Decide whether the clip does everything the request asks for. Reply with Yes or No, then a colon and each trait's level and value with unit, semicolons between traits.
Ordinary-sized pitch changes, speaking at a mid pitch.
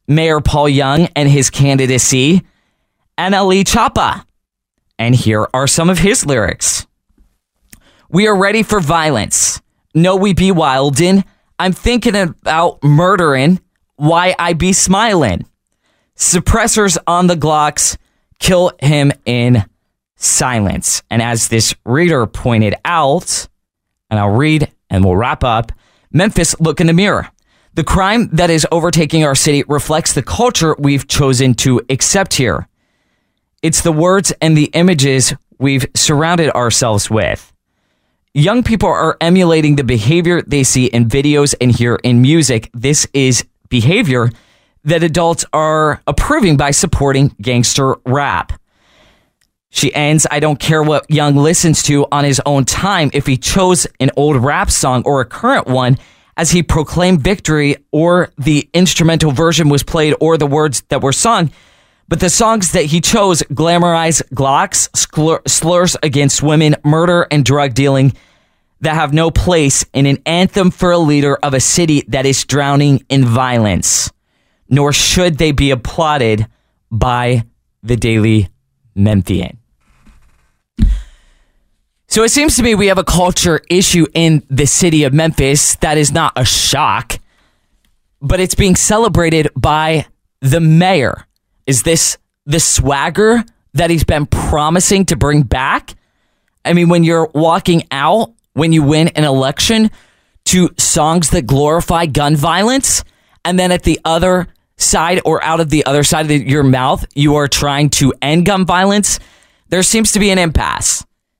Yes: average, 4.3 semitones; medium, 150 Hz